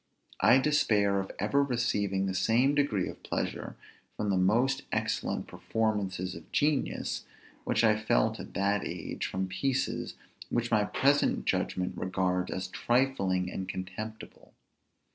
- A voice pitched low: Yes, low, 105 Hz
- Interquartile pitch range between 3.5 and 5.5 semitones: Yes, average, 4.5 semitones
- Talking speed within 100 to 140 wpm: Yes, slow, 135 wpm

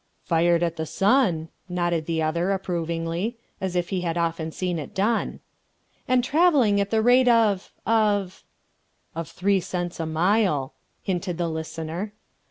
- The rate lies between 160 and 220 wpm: No, average, 150 wpm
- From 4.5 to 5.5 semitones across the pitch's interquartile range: No, average, 3.7 semitones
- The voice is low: No, medium, 180 Hz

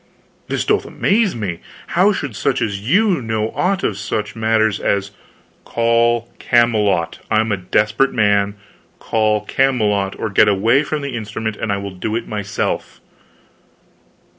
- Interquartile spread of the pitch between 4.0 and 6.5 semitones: No, average, 2.8 semitones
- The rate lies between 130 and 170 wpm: Yes, average, 155 wpm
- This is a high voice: No, low, 110 Hz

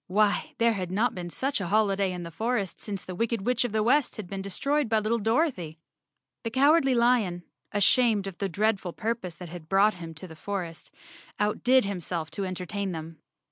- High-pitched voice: Yes, high, 200 Hz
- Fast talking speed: Yes, fast, 210 wpm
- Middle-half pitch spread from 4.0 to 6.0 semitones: Yes, average, 4.3 semitones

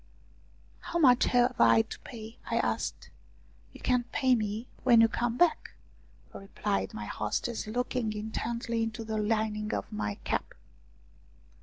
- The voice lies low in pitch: No, high, 225 Hz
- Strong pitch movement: No, narrow, 2.5 semitones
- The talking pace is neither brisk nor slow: Yes, average, 155 wpm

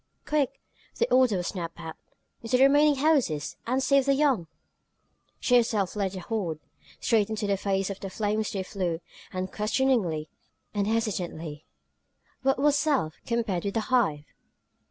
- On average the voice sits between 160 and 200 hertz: No, high, 210 Hz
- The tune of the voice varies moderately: No, wide, 5.9 semitones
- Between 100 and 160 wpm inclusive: Yes, average, 150 wpm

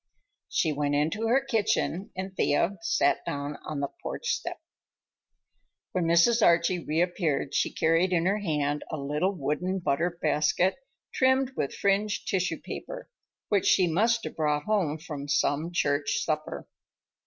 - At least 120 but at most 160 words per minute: Yes, average, 145 wpm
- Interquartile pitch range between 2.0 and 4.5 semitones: No, average, 4.9 semitones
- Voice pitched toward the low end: No, medium, 170 Hz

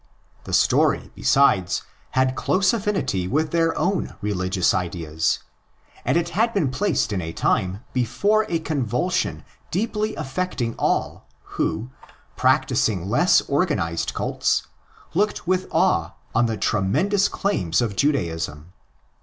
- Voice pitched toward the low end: Yes, low, 130 Hz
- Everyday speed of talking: No, slow, 120 wpm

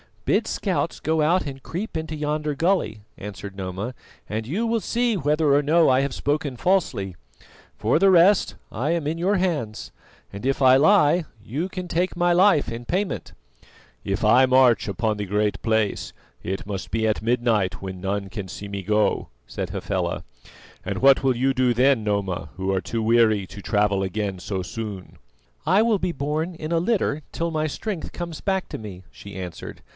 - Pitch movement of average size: No, wide, 8.1 semitones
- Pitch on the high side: No, low, 130 Hz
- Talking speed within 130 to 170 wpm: No, average, 185 wpm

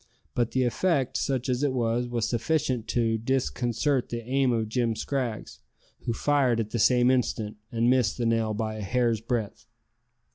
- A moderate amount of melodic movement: No, narrow, 2.3 semitones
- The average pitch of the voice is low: Yes, low, 120 Hz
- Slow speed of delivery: No, average, 175 wpm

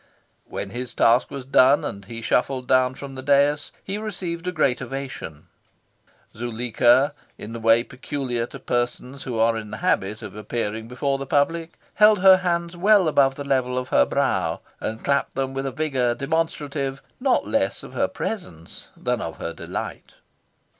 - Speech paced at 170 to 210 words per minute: Yes, average, 175 wpm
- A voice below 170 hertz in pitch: Yes, low, 135 Hz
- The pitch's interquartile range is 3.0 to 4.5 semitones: Yes, average, 3.9 semitones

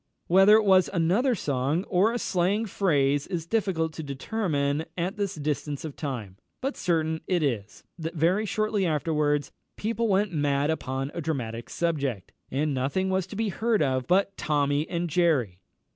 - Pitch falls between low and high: Yes, medium, 160 Hz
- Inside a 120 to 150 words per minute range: No, average, 165 wpm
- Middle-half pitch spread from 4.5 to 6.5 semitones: Yes, average, 5.2 semitones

